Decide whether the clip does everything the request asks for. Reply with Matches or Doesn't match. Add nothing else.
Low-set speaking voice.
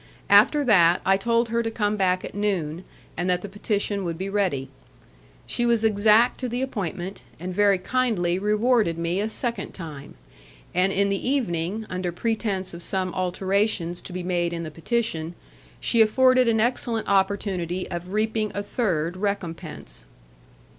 Doesn't match